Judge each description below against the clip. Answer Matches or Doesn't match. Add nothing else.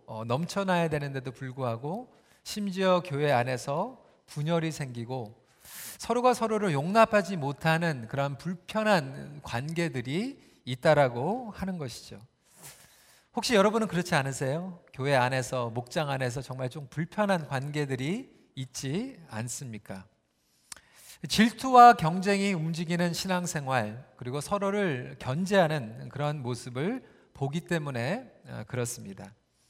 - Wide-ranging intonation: Matches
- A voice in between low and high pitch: Matches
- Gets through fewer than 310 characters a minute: Matches